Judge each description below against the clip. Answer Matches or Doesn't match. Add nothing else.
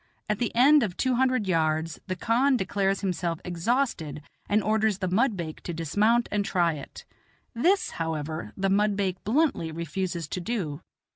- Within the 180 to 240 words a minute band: Doesn't match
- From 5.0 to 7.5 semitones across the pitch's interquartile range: Matches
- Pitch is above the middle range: Matches